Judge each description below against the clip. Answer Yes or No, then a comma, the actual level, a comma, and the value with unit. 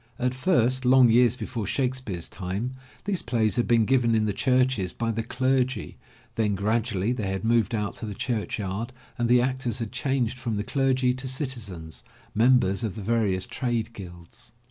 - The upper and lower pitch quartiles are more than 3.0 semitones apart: Yes, average, 3.5 semitones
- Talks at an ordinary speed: Yes, average, 180 wpm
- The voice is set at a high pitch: No, low, 115 Hz